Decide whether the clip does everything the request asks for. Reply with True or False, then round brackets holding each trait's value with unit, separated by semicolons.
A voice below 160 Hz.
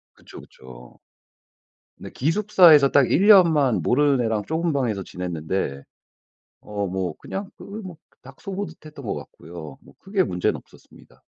True (135 Hz)